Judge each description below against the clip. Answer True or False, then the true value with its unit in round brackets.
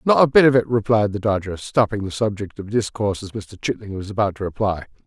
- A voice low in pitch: True (105 Hz)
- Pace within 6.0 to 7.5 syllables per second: True (6.2 syllables/s)